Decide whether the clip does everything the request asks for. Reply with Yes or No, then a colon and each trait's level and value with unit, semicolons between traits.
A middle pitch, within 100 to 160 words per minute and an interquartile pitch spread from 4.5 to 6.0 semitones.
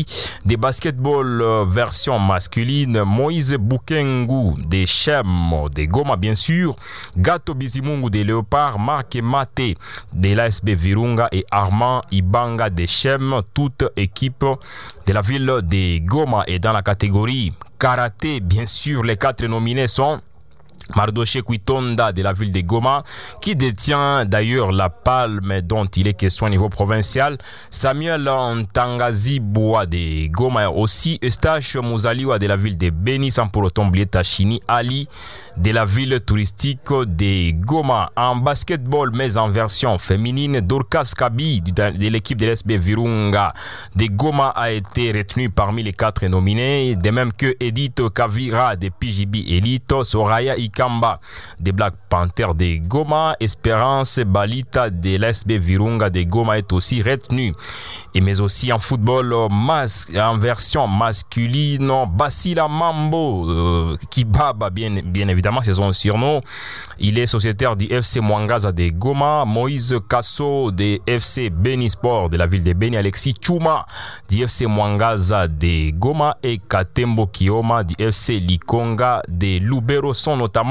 No: low, 115 Hz; average, 140 wpm; average, 4.8 semitones